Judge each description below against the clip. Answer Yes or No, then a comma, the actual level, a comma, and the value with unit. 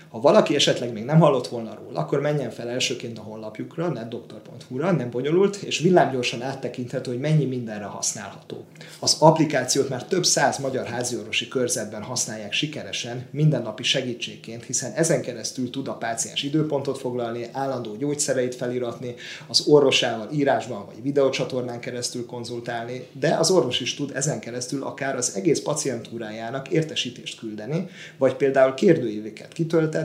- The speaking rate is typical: Yes, average, 140 wpm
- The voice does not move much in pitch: No, average, 3.3 semitones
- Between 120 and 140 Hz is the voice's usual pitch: Yes, low, 125 Hz